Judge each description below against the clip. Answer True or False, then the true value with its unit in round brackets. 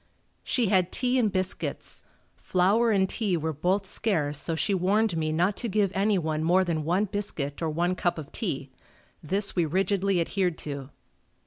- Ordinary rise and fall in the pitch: True (3.9 semitones)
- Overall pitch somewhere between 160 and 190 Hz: True (185 Hz)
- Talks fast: False (175 wpm)